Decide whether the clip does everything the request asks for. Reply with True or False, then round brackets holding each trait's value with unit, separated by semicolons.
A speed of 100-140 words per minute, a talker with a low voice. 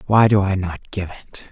False (235 wpm; 95 Hz)